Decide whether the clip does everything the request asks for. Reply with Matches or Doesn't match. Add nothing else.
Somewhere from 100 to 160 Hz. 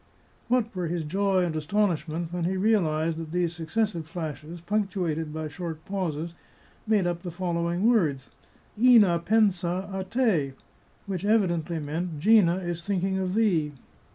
Doesn't match